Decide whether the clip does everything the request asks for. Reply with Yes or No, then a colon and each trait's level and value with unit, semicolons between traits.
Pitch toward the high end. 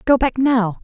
Yes: high, 245 Hz